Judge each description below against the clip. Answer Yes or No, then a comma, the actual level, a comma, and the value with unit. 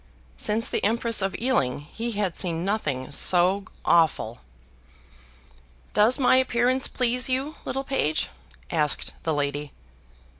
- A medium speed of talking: No, slow, 120 wpm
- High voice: Yes, high, 200 Hz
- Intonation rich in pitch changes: Yes, wide, 8.0 semitones